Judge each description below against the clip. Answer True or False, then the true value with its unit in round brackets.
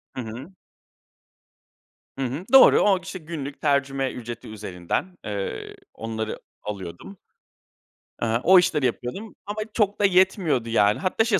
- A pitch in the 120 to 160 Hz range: True (135 Hz)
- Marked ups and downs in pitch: True (8.7 semitones)